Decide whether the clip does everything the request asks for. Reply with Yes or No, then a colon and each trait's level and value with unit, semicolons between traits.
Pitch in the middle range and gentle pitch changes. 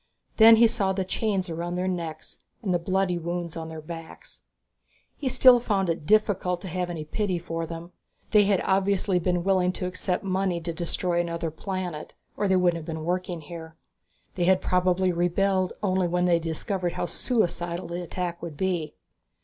Yes: medium, 180 Hz; narrow, 2.0 semitones